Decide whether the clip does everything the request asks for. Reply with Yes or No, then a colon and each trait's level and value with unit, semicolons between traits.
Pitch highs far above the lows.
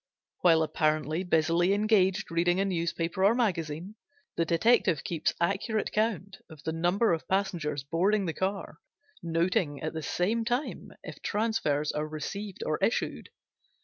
No: average, 3.9 semitones